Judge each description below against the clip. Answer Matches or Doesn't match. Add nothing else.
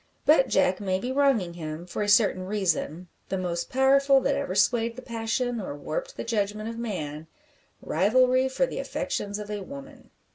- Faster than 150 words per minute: Matches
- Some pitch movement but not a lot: Doesn't match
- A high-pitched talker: Matches